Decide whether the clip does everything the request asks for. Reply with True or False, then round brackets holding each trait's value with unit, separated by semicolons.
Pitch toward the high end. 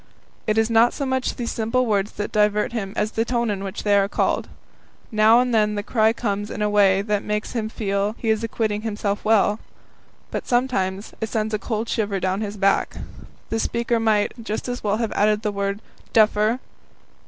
True (215 Hz)